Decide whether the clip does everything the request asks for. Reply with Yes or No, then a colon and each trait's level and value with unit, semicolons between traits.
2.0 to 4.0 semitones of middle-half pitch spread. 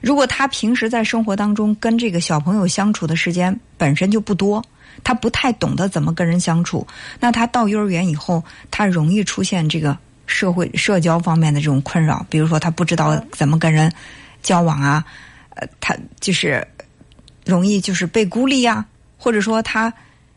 No: average, 5.2 semitones